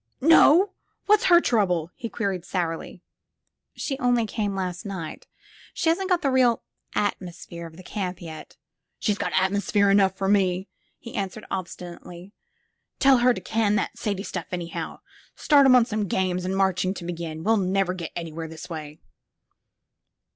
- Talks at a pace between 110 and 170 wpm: Yes, average, 165 wpm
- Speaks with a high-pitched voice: Yes, high, 195 Hz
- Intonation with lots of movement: No, average, 4.4 semitones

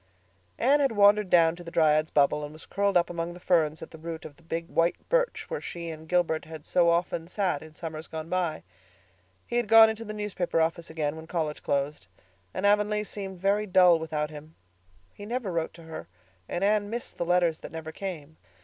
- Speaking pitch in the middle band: Yes, medium, 170 Hz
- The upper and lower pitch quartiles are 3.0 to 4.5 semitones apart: Yes, average, 4.0 semitones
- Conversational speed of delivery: No, fast, 215 wpm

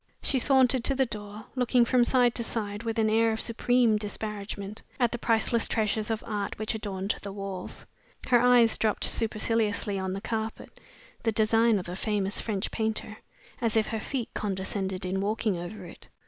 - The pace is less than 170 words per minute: No, average, 180 wpm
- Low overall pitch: No, high, 220 Hz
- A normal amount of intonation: No, narrow, 2.3 semitones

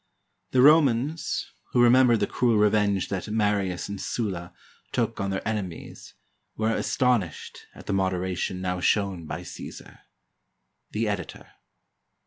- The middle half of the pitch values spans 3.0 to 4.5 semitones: Yes, average, 3.8 semitones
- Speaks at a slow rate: Yes, slow, 130 wpm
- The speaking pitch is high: No, low, 105 Hz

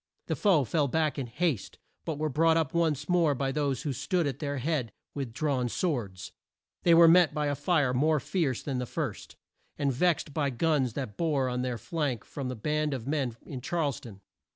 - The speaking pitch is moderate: Yes, medium, 145 Hz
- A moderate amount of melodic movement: Yes, average, 3.9 semitones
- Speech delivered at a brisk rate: Yes, fast, 210 wpm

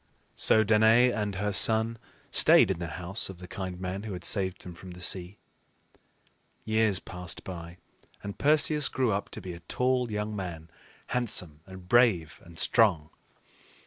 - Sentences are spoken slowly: No, average, 165 wpm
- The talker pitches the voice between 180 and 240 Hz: No, very low, 95 Hz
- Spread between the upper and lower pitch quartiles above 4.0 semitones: No, average, 3.7 semitones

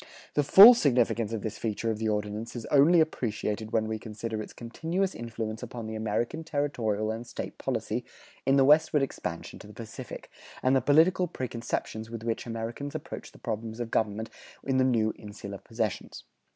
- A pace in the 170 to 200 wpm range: Yes, average, 180 wpm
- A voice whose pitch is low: Yes, low, 115 Hz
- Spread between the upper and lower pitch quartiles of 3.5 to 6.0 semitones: Yes, average, 3.9 semitones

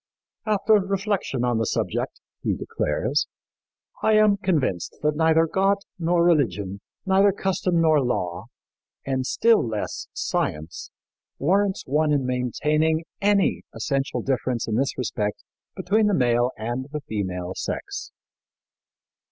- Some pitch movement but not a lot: No, wide, 7.9 semitones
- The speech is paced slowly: Yes, slow, 125 wpm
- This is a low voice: No, medium, 150 Hz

